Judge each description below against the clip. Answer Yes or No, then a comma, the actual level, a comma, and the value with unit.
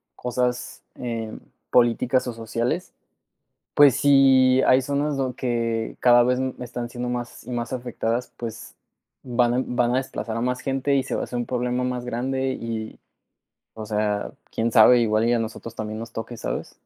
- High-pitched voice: No, low, 120 Hz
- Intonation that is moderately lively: No, narrow, 1.8 semitones